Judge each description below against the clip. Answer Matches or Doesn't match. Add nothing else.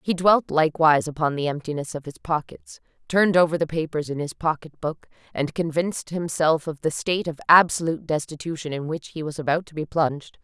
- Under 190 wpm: Doesn't match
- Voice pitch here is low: Doesn't match